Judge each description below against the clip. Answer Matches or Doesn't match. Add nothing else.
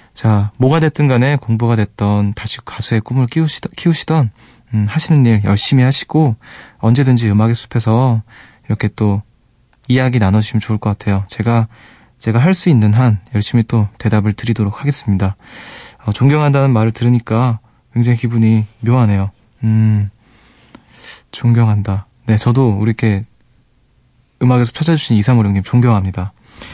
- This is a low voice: Matches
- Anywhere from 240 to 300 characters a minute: Doesn't match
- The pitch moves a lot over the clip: Doesn't match